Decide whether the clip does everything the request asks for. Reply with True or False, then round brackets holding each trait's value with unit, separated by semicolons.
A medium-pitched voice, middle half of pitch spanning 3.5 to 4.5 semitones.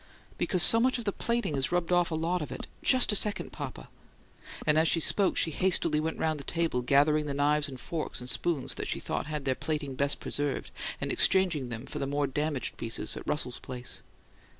True (150 Hz; 3.9 semitones)